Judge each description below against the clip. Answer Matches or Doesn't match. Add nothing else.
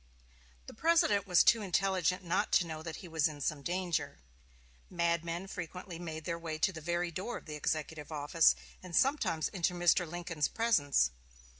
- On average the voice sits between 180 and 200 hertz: Doesn't match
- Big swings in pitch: Doesn't match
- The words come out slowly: Doesn't match